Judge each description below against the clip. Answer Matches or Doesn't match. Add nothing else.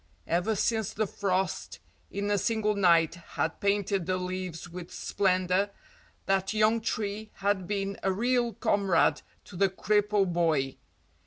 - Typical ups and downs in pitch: Doesn't match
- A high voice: Matches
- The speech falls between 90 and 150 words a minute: Matches